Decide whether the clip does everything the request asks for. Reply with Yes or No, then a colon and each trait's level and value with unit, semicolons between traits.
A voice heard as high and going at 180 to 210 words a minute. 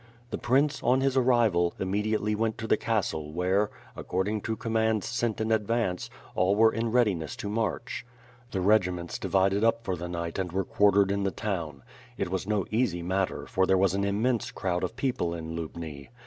No: low, 100 Hz; average, 190 wpm